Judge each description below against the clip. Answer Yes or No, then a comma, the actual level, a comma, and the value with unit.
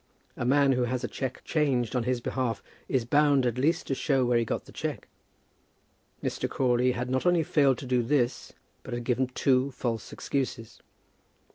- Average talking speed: Yes, average, 190 wpm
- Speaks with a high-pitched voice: No, low, 130 Hz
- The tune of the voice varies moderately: No, narrow, 2.1 semitones